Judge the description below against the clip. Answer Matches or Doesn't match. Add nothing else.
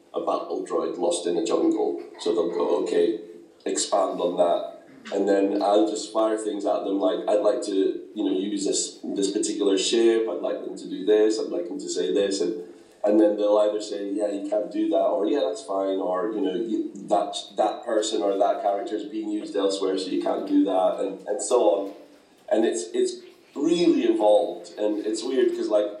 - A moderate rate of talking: Doesn't match